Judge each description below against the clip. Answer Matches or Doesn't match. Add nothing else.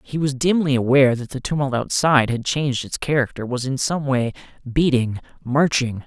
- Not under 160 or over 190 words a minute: Matches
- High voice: Doesn't match